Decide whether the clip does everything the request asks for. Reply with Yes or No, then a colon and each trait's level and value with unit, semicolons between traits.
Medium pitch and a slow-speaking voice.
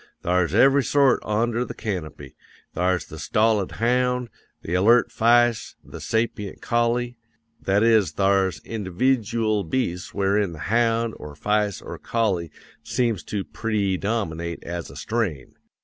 No: low, 105 Hz; slow, 130 wpm